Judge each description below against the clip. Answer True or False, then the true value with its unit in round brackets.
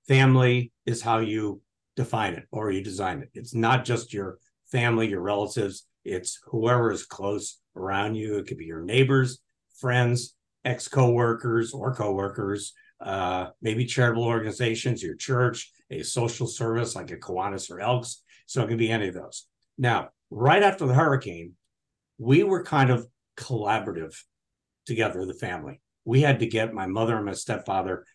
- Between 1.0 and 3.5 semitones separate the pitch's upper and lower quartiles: True (3.2 semitones)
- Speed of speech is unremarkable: True (165 wpm)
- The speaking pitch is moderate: False (115 Hz)